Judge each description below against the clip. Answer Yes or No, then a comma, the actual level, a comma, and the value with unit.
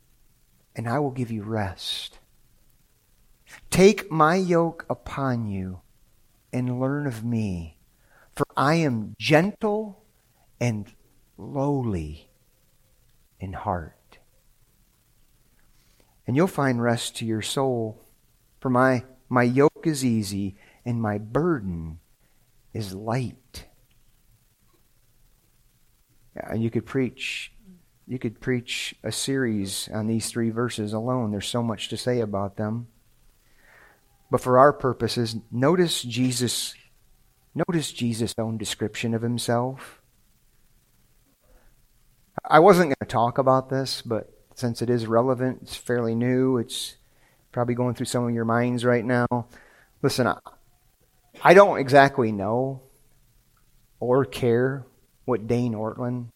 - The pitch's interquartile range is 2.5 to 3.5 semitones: Yes, average, 2.8 semitones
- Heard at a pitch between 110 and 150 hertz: Yes, low, 120 Hz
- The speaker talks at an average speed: No, slow, 120 wpm